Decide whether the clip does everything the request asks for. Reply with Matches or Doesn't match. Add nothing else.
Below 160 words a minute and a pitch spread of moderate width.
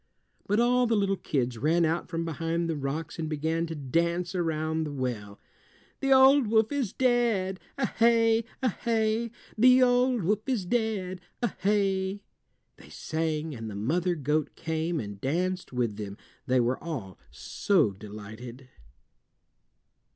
Doesn't match